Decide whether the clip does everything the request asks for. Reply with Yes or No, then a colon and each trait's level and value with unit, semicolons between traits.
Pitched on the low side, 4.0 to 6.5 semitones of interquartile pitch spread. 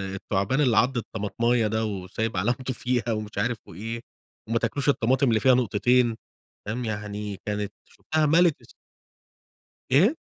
No: low, 115 Hz; average, 3.3 semitones